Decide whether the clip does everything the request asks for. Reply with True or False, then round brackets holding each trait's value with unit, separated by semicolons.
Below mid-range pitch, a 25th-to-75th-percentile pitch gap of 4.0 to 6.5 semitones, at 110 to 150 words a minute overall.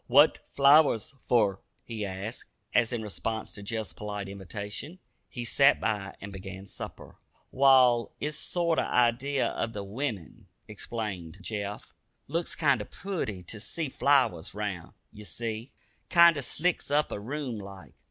True (115 Hz; 5.4 semitones; 145 wpm)